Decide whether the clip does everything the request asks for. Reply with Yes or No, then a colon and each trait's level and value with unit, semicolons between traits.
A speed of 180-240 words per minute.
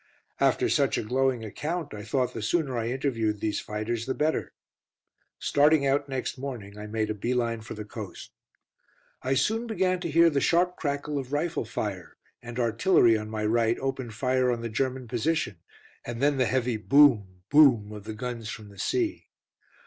Yes: average, 185 wpm